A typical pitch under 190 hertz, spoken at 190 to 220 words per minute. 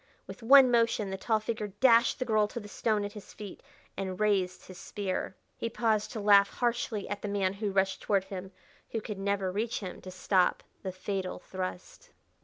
No: high, 205 Hz; average, 200 wpm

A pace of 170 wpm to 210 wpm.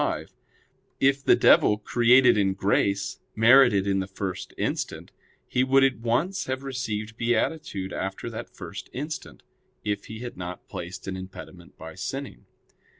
No: average, 150 wpm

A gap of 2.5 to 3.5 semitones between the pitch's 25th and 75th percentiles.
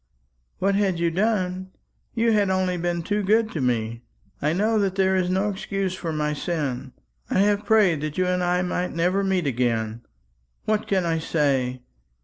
No: average, 4.4 semitones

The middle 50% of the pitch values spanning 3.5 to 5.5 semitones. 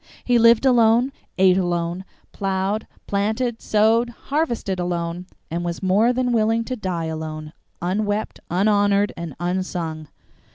Yes: average, 4.5 semitones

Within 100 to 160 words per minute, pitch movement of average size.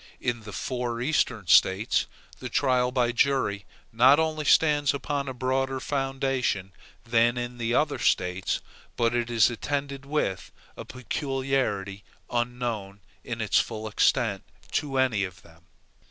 Yes: average, 140 wpm; average, 3.7 semitones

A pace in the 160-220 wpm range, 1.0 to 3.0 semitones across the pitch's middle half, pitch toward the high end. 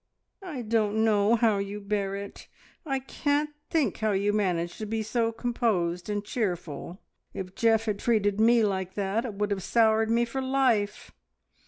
Yes: average, 170 wpm; narrow, 2.6 semitones; high, 215 Hz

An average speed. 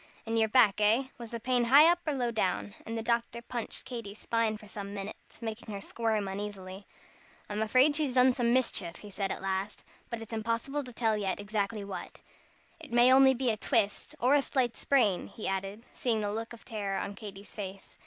No: fast, 210 wpm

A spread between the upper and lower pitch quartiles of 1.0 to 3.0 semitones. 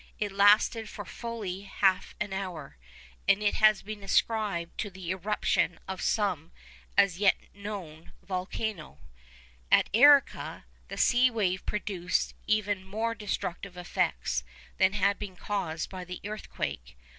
Yes: narrow, 2.6 semitones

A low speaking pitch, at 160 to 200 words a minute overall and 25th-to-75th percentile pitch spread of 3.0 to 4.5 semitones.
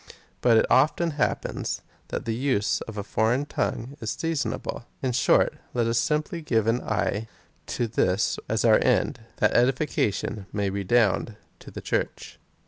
Yes: low, 115 Hz; average, 165 wpm; average, 3.5 semitones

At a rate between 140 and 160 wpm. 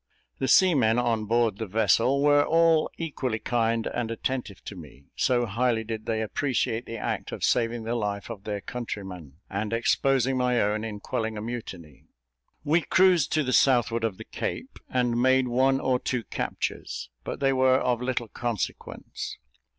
No: average, 170 wpm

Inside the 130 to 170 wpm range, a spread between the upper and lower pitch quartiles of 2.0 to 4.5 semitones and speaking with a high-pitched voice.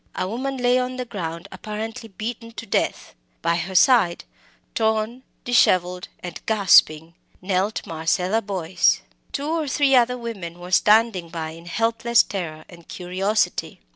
No: average, 140 wpm; average, 4.9 semitones; high, 205 Hz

